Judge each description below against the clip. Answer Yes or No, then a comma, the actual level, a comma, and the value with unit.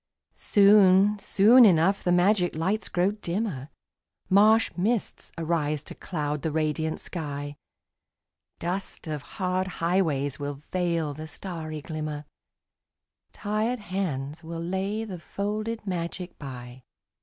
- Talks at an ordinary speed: No, slow, 115 wpm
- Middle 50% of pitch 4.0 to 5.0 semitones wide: Yes, average, 4.5 semitones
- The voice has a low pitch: No, medium, 175 Hz